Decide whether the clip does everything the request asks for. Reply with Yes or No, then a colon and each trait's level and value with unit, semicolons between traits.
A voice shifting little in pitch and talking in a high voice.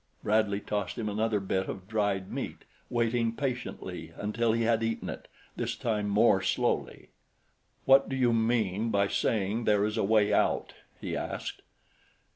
No: narrow, 2.2 semitones; low, 110 Hz